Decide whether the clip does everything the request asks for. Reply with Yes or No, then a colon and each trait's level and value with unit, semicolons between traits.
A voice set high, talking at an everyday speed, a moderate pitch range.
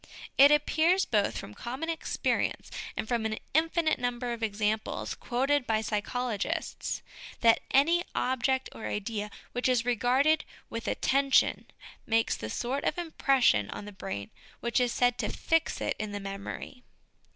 Yes: high, 245 Hz; average, 150 wpm; average, 4.2 semitones